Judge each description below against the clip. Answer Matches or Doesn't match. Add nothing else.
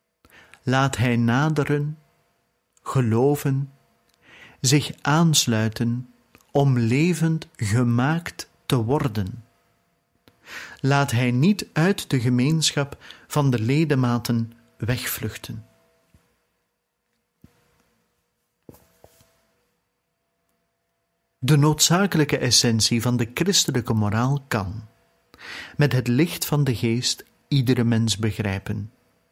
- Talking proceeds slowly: Matches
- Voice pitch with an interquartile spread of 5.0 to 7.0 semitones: Doesn't match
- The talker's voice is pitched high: Doesn't match